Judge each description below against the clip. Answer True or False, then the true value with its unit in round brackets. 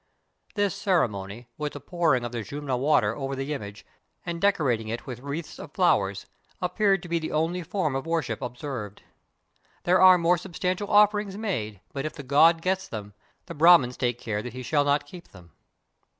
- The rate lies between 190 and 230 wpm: True (195 wpm)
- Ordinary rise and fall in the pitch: False (6.5 semitones)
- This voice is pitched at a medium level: True (145 Hz)